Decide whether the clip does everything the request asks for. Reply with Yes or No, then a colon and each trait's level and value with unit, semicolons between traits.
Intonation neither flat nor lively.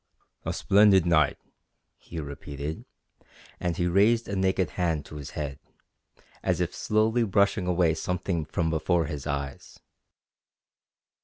Yes: average, 4.1 semitones